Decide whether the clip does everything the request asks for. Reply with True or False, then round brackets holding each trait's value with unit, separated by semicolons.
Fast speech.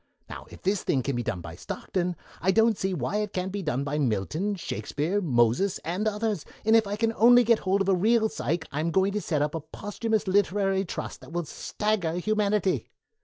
True (215 wpm)